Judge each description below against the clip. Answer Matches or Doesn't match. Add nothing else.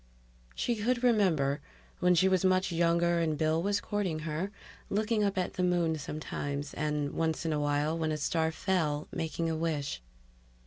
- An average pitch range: Matches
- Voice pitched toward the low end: Doesn't match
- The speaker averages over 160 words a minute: Matches